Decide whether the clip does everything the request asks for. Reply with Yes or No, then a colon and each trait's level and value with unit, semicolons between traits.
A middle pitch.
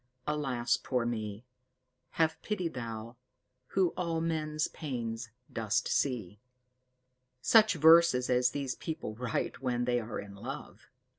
No: low, 125 Hz